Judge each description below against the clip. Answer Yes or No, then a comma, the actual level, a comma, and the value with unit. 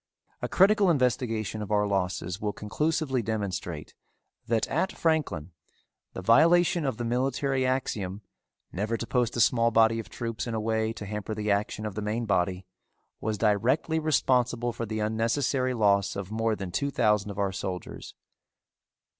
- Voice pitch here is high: No, low, 110 Hz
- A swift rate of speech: No, average, 165 wpm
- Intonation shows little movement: No, average, 3.6 semitones